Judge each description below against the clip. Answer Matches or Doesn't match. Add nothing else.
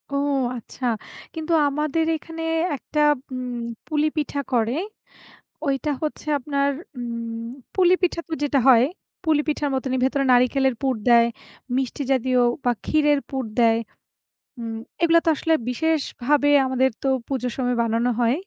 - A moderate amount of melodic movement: Matches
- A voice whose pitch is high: Matches